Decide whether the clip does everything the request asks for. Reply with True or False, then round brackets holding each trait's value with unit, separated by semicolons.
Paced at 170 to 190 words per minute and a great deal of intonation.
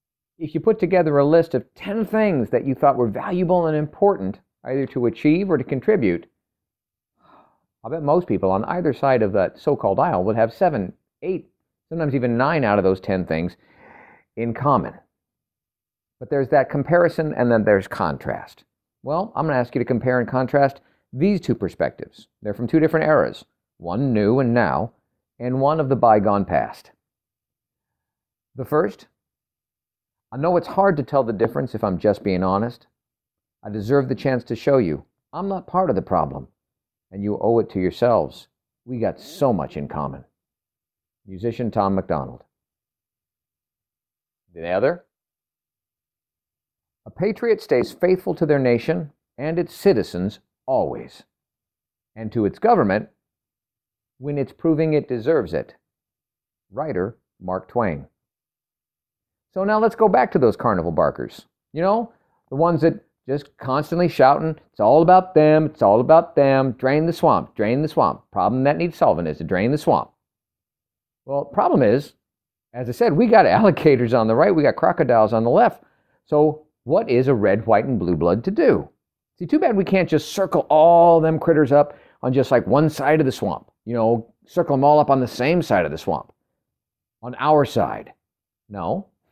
True (175 wpm; 6.2 semitones)